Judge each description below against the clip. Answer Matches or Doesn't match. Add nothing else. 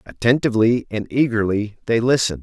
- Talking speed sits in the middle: Doesn't match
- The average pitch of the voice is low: Matches